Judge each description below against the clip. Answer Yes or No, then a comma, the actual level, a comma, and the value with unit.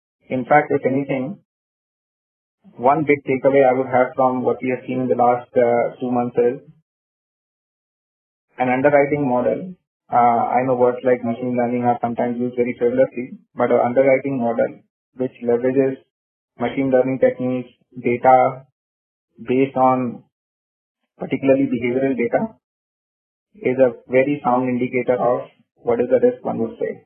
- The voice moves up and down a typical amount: No, narrow, 1.6 semitones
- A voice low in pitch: Yes, low, 125 Hz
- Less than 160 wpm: Yes, average, 145 wpm